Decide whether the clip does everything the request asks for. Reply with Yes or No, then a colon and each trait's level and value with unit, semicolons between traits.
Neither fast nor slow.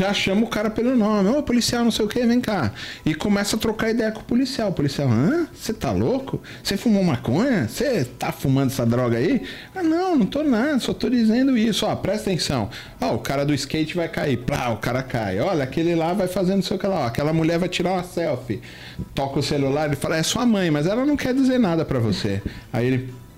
No: fast, 250 wpm